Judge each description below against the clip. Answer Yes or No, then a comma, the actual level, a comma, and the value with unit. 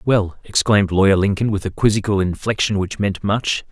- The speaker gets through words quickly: No, average, 180 wpm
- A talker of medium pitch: No, low, 100 Hz